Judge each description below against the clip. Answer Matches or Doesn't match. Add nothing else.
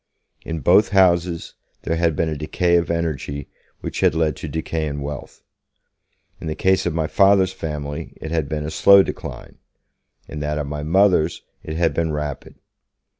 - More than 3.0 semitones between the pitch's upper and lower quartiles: Doesn't match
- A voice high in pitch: Doesn't match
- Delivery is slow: Doesn't match